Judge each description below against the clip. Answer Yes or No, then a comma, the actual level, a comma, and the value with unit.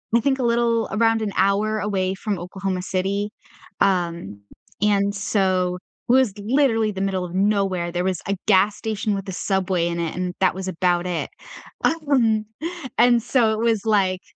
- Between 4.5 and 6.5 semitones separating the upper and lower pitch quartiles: No, average, 2.9 semitones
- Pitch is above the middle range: Yes, high, 195 Hz